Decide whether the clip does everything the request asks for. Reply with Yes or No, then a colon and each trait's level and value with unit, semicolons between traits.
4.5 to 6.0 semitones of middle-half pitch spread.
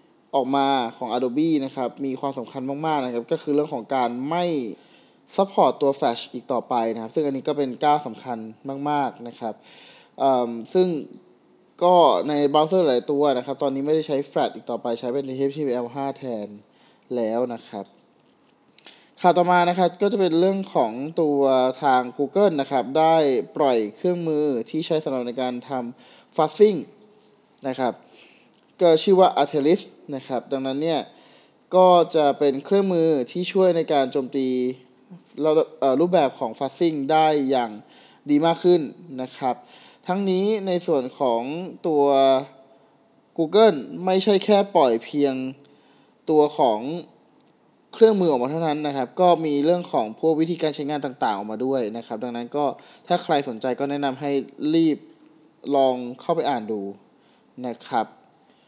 Yes: average, 5.1 semitones